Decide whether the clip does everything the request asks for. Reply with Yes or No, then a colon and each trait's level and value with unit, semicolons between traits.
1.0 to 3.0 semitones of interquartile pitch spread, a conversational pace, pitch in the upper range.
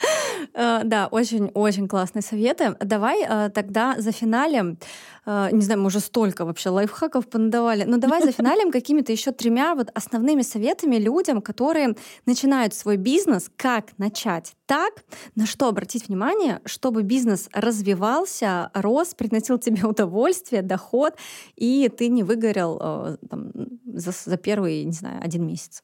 No: average, 3.7 semitones; average, 135 wpm; high, 225 Hz